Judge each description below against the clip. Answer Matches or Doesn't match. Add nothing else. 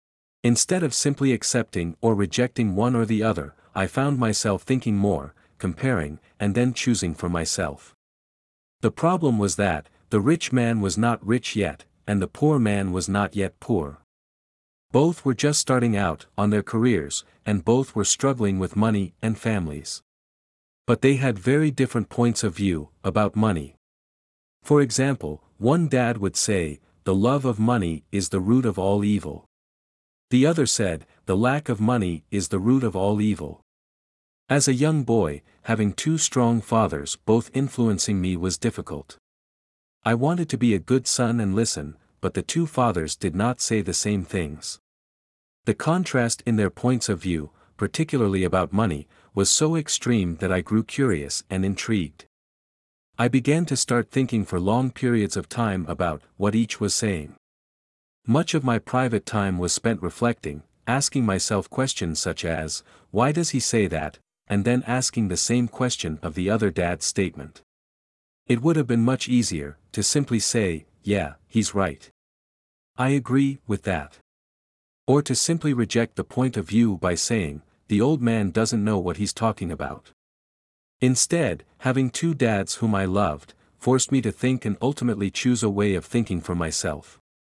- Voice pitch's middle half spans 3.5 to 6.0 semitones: Matches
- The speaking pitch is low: Matches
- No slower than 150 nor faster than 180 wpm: Matches